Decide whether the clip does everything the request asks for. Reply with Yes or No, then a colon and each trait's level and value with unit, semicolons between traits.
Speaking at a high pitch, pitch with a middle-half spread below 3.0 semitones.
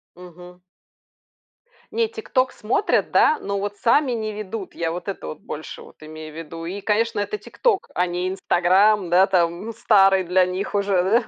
No: high, 195 Hz; average, 3.4 semitones